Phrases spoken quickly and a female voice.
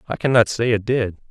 No: fast, 230 wpm; male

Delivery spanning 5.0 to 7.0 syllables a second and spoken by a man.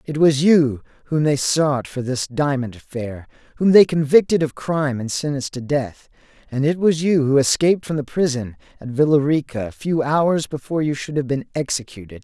Yes: 5.3 syllables/s; male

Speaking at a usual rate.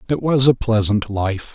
Yes: average, 195 wpm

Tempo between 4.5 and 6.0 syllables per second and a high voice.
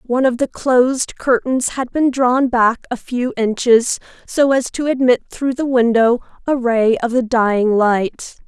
No: 4.1 syllables/s; high, 245 Hz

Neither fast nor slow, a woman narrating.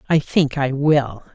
Yes: average, 180 wpm; female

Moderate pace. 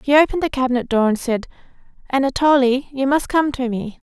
Yes: average, 190 wpm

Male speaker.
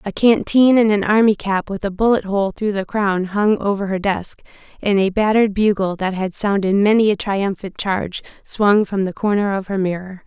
No: female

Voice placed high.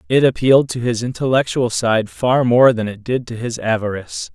No: low, 120 Hz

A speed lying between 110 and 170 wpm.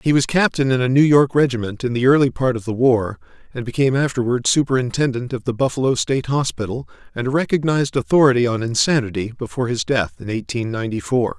No: average, 195 wpm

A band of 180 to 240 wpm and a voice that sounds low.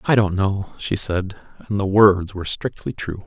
Yes: average, 200 wpm; very low, 95 Hz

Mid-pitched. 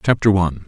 No: very low, 95 Hz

